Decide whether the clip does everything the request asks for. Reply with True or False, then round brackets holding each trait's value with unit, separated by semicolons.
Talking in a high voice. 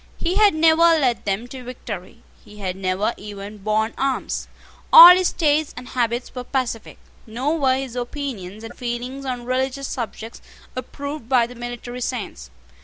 True (245 Hz)